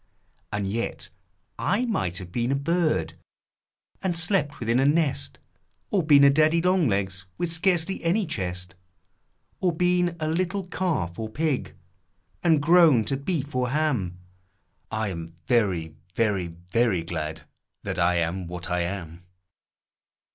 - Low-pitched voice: Yes, low, 130 Hz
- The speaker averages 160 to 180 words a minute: No, average, 140 wpm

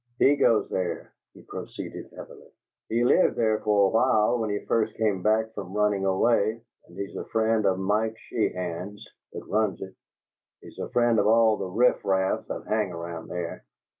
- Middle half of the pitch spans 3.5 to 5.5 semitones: No, average, 2.8 semitones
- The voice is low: Yes, low, 105 Hz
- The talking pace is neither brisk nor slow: Yes, average, 180 wpm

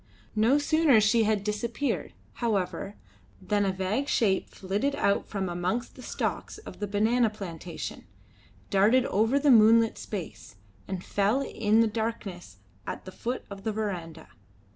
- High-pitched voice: Yes, high, 210 Hz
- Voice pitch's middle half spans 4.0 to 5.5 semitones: No, average, 3.3 semitones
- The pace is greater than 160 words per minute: No, average, 145 wpm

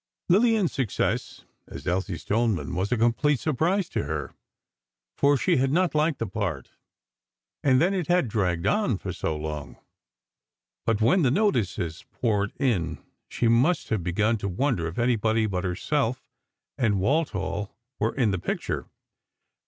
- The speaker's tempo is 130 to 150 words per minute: Yes, average, 145 wpm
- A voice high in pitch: No, low, 115 Hz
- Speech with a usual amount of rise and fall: No, wide, 7.4 semitones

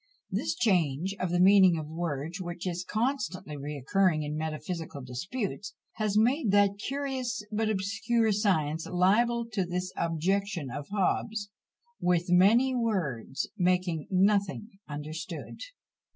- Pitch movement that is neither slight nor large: Yes, average, 4.6 semitones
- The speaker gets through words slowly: Yes, slow, 125 wpm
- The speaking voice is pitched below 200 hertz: Yes, medium, 185 Hz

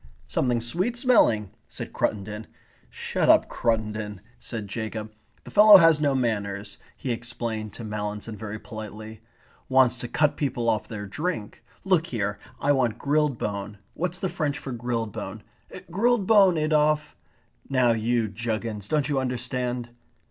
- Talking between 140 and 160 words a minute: Yes, average, 145 wpm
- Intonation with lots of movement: Yes, wide, 5.7 semitones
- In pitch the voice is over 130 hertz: No, low, 120 Hz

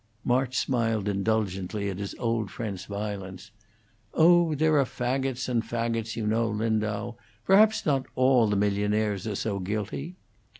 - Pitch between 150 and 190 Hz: No, low, 110 Hz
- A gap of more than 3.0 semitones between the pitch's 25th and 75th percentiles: Yes, average, 3.7 semitones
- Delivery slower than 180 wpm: Yes, average, 140 wpm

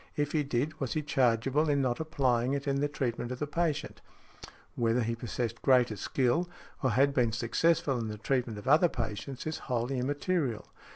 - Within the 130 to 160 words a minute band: No, average, 190 wpm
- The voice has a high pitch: No, low, 130 Hz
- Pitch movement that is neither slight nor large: Yes, average, 3.6 semitones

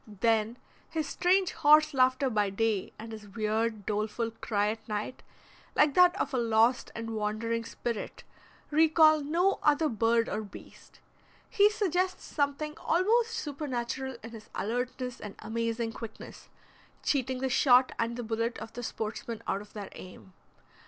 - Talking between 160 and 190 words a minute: No, average, 150 wpm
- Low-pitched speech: No, high, 235 Hz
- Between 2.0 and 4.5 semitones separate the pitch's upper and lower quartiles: No, average, 5.0 semitones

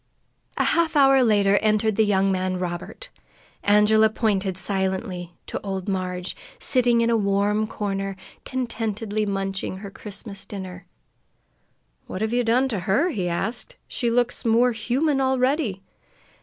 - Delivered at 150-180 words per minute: No, average, 140 wpm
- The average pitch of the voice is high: Yes, high, 210 Hz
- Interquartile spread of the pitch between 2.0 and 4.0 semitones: Yes, average, 3.6 semitones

